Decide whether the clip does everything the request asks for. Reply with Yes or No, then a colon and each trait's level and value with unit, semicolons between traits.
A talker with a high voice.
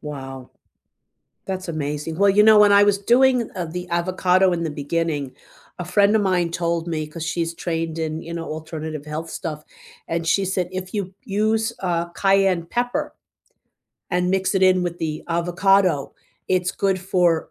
No: medium, 175 Hz